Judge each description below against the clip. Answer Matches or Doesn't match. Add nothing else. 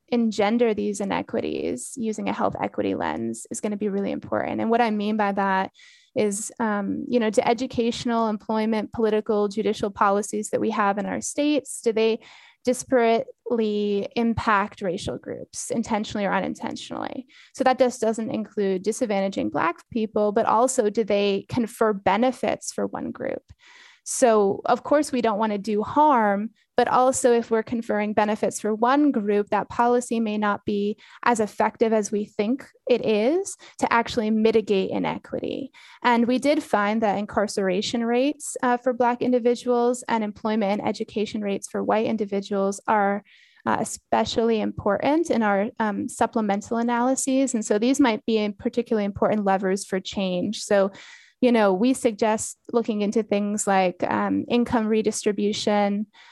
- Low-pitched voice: Doesn't match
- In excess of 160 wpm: Doesn't match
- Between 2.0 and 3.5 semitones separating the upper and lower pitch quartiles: Matches